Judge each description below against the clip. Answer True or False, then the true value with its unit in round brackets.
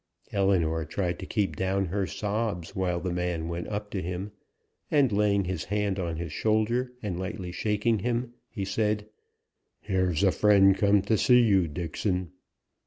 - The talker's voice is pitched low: True (100 Hz)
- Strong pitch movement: False (2.8 semitones)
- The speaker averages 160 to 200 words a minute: True (165 wpm)